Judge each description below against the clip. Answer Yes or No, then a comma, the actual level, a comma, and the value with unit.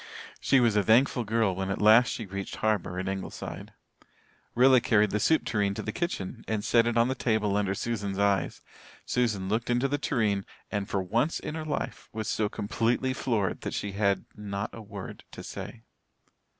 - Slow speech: No, average, 190 wpm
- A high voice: No, low, 110 Hz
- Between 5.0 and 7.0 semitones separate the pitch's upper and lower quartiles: No, average, 3.1 semitones